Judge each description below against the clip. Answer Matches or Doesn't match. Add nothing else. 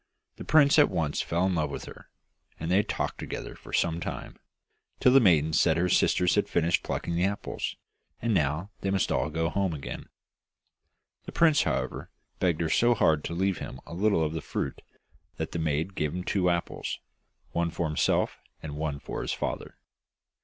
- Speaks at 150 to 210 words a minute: Matches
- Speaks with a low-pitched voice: Matches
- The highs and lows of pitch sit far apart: Doesn't match